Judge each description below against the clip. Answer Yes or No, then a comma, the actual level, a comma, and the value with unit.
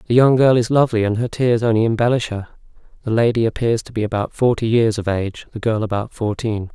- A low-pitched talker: Yes, low, 115 Hz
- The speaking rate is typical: No, fast, 220 wpm